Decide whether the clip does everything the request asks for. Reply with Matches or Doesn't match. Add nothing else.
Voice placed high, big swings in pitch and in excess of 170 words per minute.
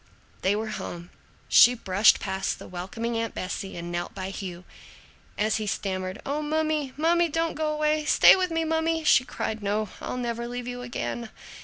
Matches